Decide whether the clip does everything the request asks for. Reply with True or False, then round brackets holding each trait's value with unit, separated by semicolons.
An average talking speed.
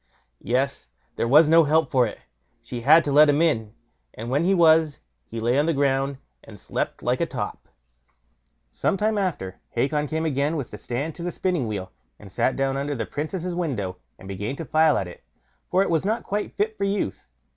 False (210 wpm)